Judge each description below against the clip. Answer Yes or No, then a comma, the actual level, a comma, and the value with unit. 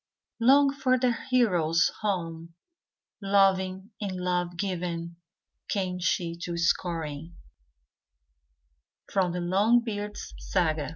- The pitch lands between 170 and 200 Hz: Yes, medium, 185 Hz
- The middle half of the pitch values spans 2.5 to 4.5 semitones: Yes, average, 3.4 semitones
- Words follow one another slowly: Yes, slow, 95 wpm